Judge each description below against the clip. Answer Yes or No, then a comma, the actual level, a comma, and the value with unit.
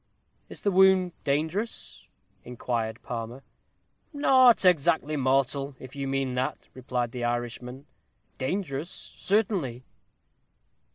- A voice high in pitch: No, low, 135 Hz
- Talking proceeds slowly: Yes, slow, 100 wpm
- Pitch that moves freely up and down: Yes, wide, 6.6 semitones